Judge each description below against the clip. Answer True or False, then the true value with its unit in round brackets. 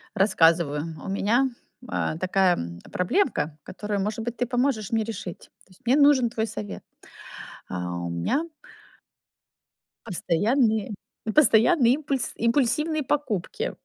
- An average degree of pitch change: False (6.5 semitones)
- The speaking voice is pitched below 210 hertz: False (220 Hz)